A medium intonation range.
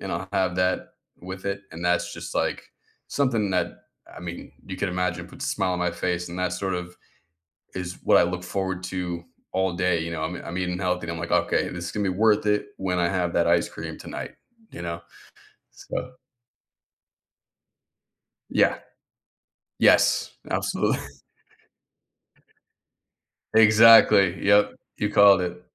No: narrow, 1.8 semitones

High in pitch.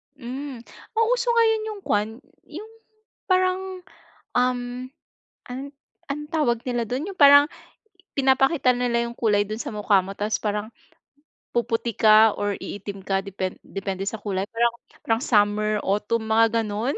Yes: high, 235 Hz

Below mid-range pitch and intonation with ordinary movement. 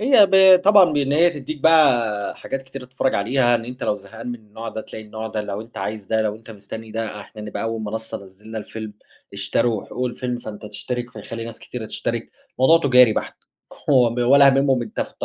Yes: low, 115 Hz; average, 3.5 semitones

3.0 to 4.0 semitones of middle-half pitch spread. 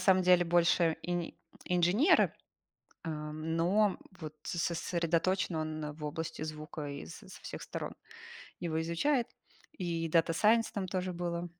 No: narrow, 2.4 semitones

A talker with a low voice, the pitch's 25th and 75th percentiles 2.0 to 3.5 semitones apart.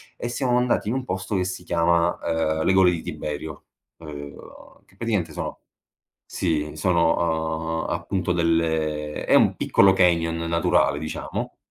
Yes: very low, 85 Hz; average, 2.7 semitones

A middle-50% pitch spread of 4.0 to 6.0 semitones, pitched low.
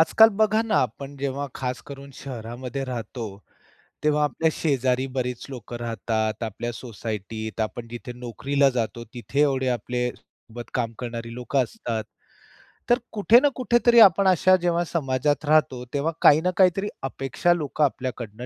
Yes: average, 4.4 semitones; low, 130 Hz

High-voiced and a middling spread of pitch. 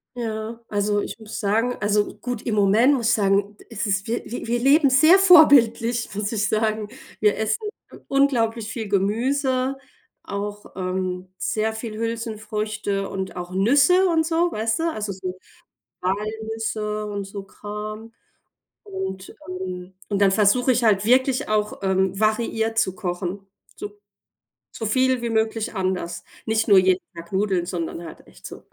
Yes: high, 215 Hz; average, 3.1 semitones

